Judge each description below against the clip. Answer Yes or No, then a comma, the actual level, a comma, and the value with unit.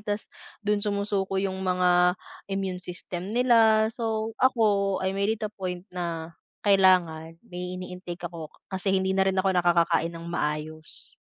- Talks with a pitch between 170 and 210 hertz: Yes, high, 190 Hz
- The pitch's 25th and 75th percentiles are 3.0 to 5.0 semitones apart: No, narrow, 2.4 semitones